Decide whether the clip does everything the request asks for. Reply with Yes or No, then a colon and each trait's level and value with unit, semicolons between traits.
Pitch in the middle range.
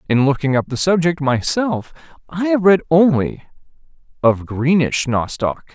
Yes: medium, 150 Hz